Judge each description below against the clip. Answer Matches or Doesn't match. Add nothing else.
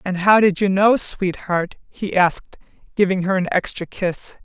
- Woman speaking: Matches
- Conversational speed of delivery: Matches